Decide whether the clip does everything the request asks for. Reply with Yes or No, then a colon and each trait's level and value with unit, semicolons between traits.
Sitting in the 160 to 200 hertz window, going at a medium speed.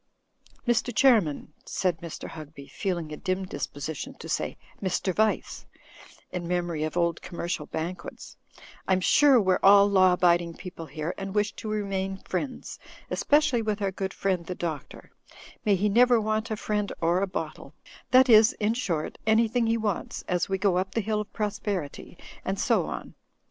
Yes: high, 190 Hz; average, 175 wpm